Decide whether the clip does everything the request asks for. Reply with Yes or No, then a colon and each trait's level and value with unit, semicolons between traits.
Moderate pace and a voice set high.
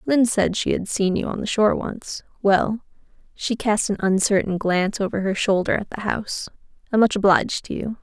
Yes: average, 185 wpm; high, 205 Hz